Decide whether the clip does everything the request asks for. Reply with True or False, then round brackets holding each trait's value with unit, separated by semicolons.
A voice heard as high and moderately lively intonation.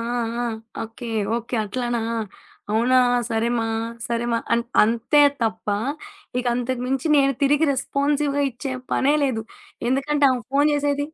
True (255 Hz; 3.2 semitones)